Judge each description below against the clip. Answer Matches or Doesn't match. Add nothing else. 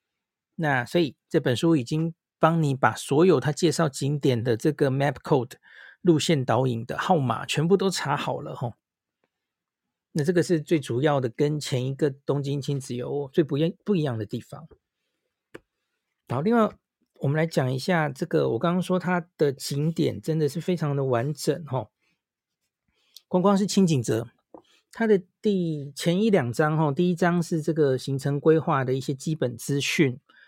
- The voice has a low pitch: Doesn't match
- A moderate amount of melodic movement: Matches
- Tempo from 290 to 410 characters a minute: Doesn't match